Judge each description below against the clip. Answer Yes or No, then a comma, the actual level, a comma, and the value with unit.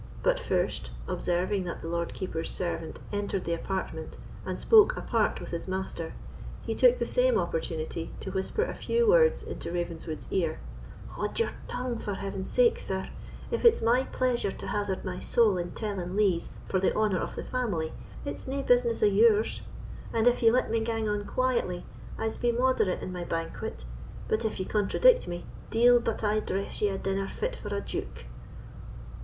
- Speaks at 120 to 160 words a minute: No, average, 185 wpm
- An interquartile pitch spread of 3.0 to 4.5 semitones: No, average, 5.1 semitones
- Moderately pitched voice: No, high, 205 Hz